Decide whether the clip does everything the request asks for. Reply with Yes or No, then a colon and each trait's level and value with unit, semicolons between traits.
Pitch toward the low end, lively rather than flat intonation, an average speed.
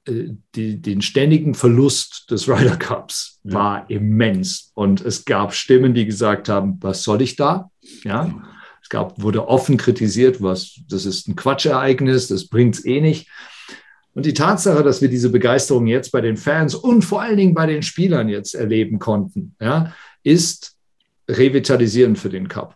Yes: low, 125 Hz; wide, 5.7 semitones; average, 165 wpm